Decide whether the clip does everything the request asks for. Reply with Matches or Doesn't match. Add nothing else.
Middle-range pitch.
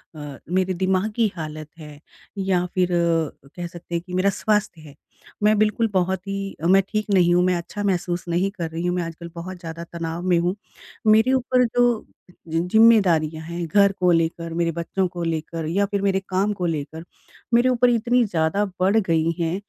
Matches